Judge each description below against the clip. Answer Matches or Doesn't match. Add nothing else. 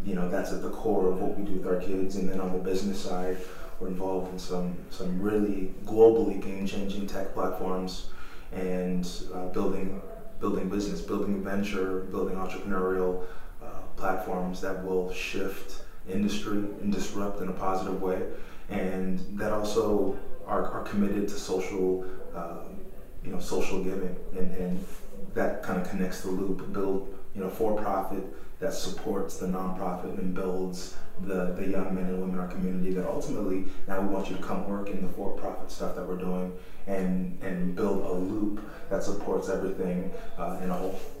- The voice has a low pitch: Matches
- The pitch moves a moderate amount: Doesn't match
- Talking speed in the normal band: Matches